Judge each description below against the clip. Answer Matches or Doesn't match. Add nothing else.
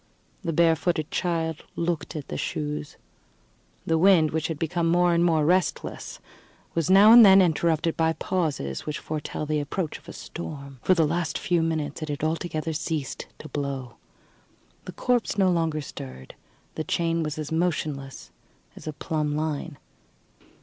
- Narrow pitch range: Matches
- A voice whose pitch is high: Doesn't match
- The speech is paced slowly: Doesn't match